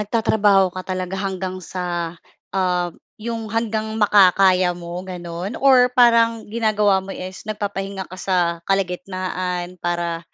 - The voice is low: No, high, 190 Hz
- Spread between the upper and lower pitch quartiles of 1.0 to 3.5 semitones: Yes, average, 2.9 semitones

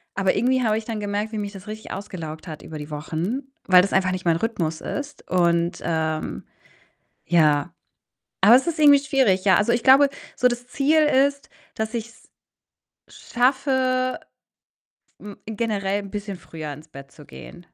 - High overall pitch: Yes, high, 205 Hz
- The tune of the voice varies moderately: No, wide, 6.6 semitones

